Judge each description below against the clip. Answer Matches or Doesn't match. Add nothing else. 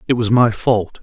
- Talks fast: Matches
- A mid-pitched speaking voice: Doesn't match